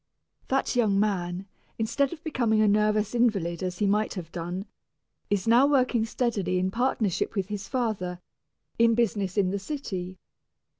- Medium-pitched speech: No, high, 210 Hz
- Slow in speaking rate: No, average, 155 wpm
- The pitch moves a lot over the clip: No, average, 3.9 semitones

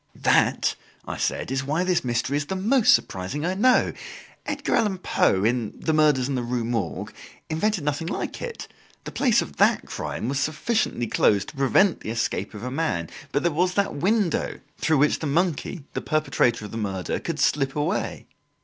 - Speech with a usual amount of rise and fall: No, wide, 7.0 semitones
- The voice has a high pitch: No, medium, 150 Hz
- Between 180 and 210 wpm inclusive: Yes, average, 190 wpm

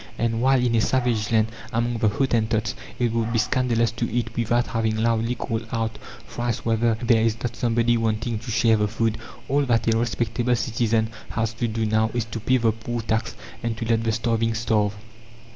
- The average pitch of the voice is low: Yes, low, 115 Hz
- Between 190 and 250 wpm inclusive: Yes, average, 200 wpm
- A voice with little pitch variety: Yes, narrow, 1.1 semitones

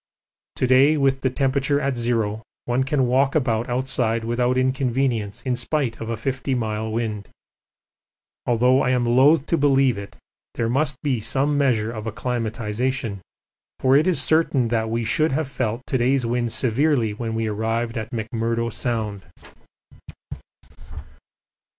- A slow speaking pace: No, average, 150 wpm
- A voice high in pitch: No, low, 125 Hz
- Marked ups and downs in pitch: No, average, 3.0 semitones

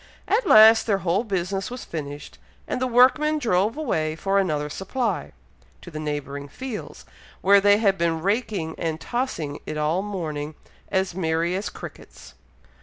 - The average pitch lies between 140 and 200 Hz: Yes, high, 190 Hz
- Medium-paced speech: Yes, average, 155 wpm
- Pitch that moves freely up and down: Yes, wide, 5.8 semitones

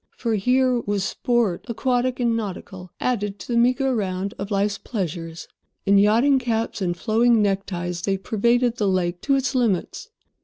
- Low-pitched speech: No, high, 215 Hz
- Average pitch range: Yes, average, 4.1 semitones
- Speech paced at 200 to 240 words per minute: No, average, 160 wpm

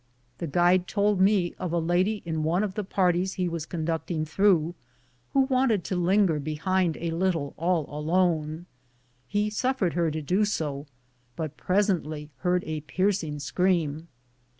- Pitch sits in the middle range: Yes, medium, 175 Hz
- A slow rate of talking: No, average, 155 wpm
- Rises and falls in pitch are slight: No, average, 3.3 semitones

